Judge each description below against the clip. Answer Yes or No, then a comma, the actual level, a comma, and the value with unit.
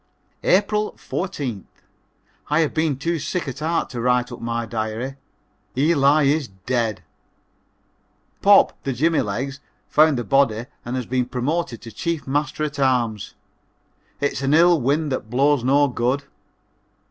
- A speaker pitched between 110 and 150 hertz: Yes, low, 135 Hz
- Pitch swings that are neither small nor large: Yes, average, 3.9 semitones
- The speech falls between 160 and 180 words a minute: No, average, 145 wpm